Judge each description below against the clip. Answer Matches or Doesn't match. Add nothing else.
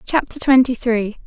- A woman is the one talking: Matches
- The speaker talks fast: Doesn't match